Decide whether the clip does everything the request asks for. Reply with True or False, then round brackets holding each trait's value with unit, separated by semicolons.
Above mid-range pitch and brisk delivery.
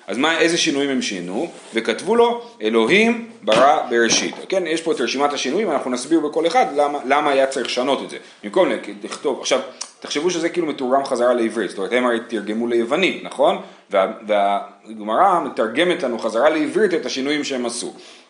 False (140 Hz; 175 wpm)